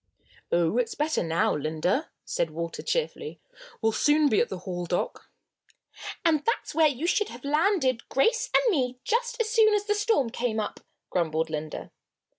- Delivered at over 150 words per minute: Yes, average, 170 wpm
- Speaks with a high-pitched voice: Yes, very high, 270 Hz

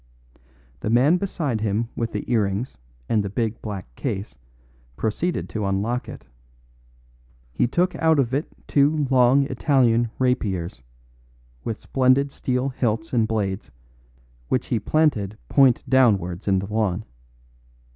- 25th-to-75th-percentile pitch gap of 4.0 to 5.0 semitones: Yes, average, 4.4 semitones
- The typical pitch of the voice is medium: No, low, 115 Hz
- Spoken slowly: Yes, slow, 130 wpm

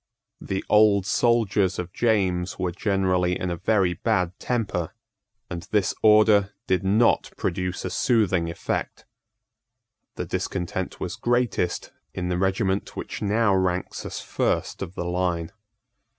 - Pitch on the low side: Yes, very low, 95 Hz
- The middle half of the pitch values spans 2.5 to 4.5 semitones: Yes, average, 2.8 semitones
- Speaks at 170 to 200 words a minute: No, slow, 135 wpm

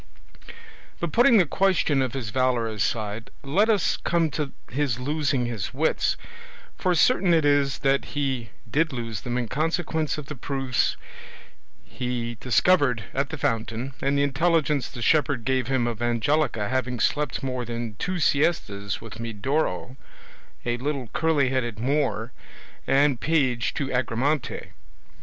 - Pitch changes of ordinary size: Yes, average, 4.0 semitones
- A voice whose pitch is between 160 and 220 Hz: No, low, 135 Hz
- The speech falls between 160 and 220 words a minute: No, average, 145 wpm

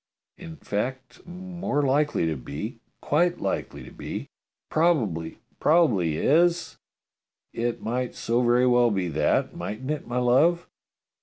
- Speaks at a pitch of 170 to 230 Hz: No, low, 125 Hz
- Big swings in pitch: Yes, wide, 6.5 semitones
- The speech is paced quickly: No, average, 140 wpm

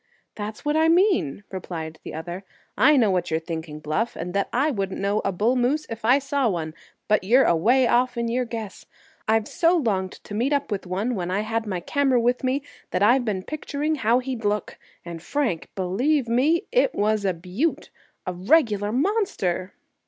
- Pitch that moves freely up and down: Yes, wide, 6.1 semitones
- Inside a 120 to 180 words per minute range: No, average, 190 wpm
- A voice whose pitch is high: Yes, high, 220 Hz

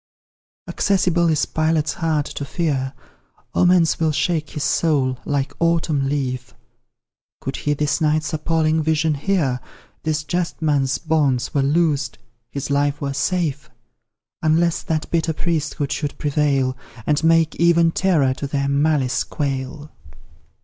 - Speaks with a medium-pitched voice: Yes, medium, 150 Hz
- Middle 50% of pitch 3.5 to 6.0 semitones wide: No, narrow, 2.6 semitones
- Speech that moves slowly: Yes, slow, 130 wpm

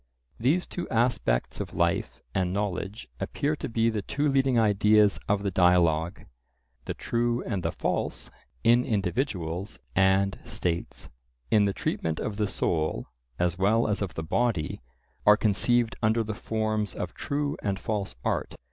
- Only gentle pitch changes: No, average, 3.8 semitones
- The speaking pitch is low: Yes, low, 105 Hz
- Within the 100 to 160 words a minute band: Yes, average, 155 wpm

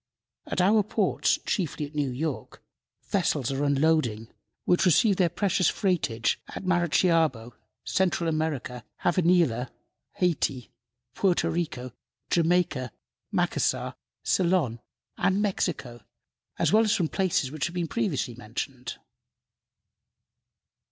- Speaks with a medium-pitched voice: Yes, medium, 160 Hz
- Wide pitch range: Yes, wide, 5.9 semitones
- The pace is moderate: No, slow, 110 wpm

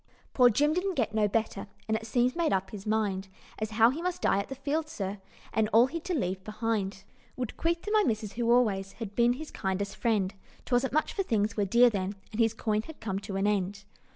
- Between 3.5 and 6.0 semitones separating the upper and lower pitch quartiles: Yes, average, 4.0 semitones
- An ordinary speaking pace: No, fast, 235 wpm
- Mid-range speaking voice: No, high, 220 Hz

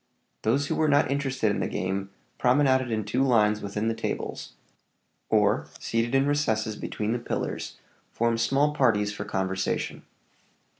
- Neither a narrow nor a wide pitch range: Yes, average, 4.2 semitones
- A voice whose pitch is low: Yes, low, 115 Hz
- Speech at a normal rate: Yes, average, 150 wpm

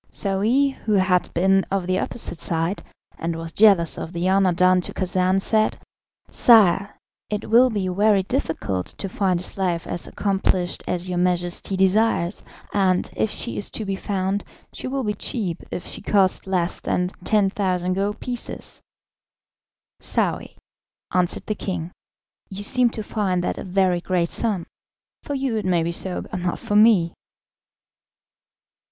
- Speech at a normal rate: Yes, average, 160 wpm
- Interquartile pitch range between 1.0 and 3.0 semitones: Yes, average, 2.7 semitones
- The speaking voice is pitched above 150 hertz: Yes, high, 190 Hz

